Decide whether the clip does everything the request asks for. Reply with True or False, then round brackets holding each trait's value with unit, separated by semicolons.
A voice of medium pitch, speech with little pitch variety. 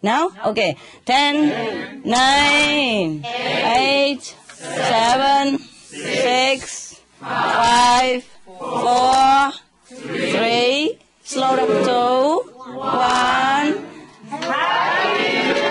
False (260 Hz; 2.0 semitones)